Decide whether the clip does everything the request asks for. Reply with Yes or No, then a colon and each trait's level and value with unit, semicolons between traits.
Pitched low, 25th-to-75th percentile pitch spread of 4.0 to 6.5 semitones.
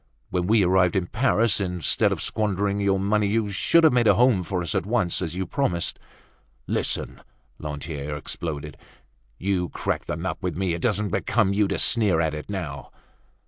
No: very low, 95 Hz; average, 3.6 semitones